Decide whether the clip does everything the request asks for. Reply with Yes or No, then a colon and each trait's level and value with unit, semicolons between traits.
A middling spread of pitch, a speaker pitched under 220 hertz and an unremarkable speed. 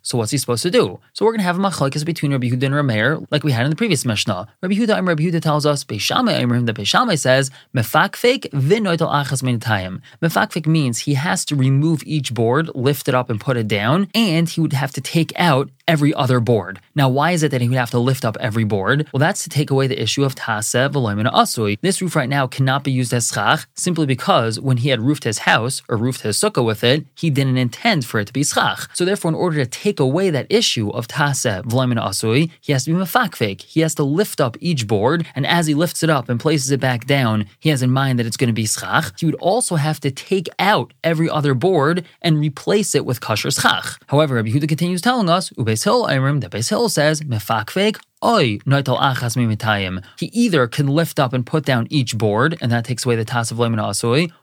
No: average, 5.0 semitones; medium, 140 Hz; fast, 230 wpm